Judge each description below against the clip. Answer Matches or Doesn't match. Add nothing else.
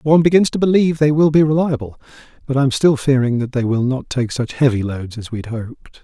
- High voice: Doesn't match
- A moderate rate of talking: Doesn't match